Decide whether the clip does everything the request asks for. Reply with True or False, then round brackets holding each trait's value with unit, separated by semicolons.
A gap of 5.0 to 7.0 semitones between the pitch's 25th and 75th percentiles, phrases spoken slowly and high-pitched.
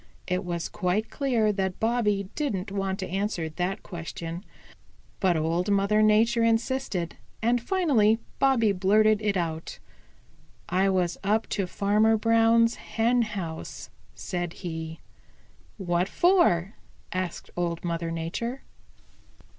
False (4.2 semitones; 120 wpm; 200 Hz)